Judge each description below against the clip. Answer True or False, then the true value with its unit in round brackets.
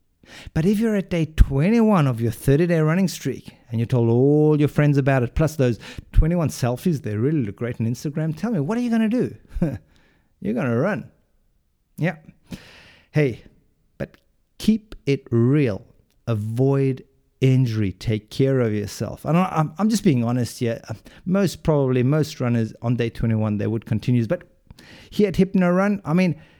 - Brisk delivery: False (180 wpm)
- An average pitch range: False (6.6 semitones)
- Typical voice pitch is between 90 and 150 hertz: True (135 Hz)